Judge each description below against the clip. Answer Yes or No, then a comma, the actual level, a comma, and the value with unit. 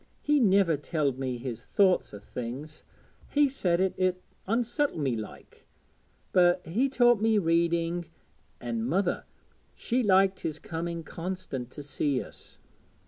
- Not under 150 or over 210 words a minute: No, average, 140 wpm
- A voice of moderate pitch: Yes, medium, 170 Hz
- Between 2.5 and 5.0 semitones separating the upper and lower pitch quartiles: No, wide, 5.6 semitones